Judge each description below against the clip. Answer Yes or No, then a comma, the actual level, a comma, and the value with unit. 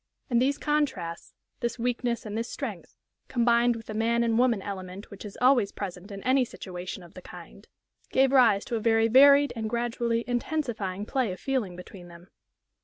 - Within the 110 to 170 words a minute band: No, average, 180 wpm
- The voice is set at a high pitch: Yes, high, 230 Hz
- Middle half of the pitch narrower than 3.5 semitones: No, average, 3.8 semitones